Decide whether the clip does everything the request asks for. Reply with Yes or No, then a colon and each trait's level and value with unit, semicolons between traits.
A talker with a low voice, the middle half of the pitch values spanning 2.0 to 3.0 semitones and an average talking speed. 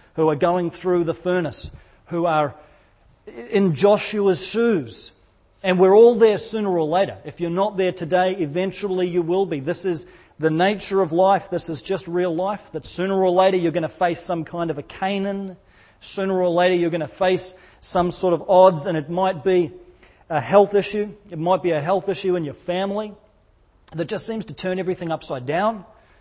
No: medium, 180 Hz; narrow, 2.5 semitones; average, 195 wpm